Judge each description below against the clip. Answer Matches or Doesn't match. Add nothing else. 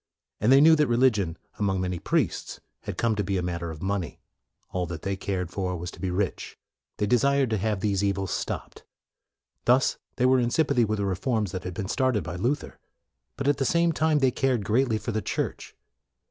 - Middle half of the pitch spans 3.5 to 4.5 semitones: Doesn't match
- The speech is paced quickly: Matches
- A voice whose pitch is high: Doesn't match